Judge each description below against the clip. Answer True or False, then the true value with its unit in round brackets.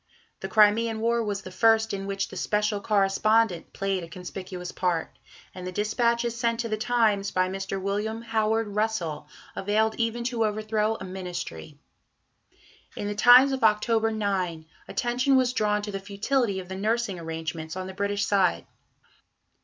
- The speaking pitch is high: True (210 Hz)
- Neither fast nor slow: True (160 wpm)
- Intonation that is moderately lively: True (3.0 semitones)